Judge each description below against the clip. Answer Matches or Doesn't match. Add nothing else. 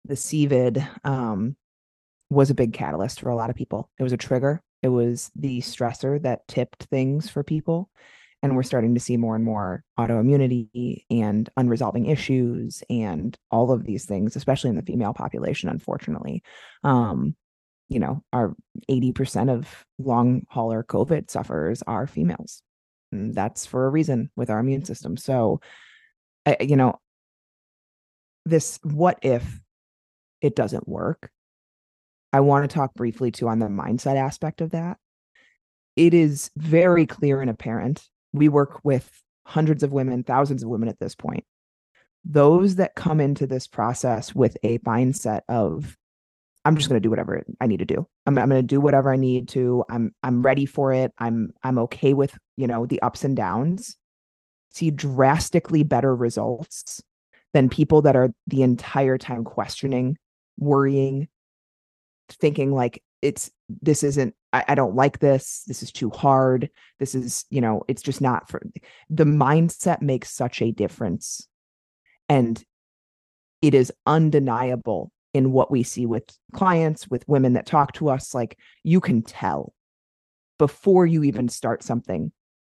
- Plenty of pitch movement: Doesn't match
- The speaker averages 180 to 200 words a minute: Doesn't match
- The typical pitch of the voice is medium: Doesn't match